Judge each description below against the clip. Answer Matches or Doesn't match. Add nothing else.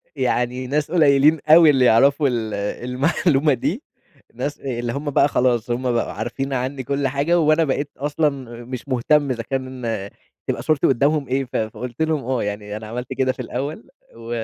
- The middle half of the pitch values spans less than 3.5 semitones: Matches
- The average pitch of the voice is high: Doesn't match